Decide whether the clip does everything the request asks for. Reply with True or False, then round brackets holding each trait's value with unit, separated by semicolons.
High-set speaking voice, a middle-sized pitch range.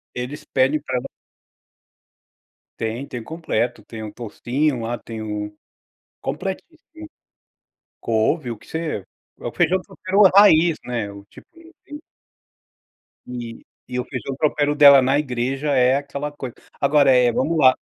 False (135 Hz; 4.2 semitones)